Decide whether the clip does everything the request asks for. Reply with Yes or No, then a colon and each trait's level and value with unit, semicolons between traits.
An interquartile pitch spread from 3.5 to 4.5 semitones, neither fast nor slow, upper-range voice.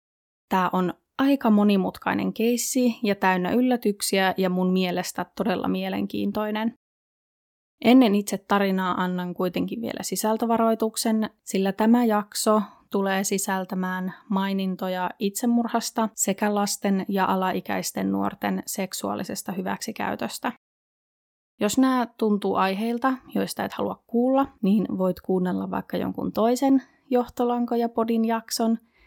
Yes: average, 3.8 semitones; average, 105 wpm; high, 205 Hz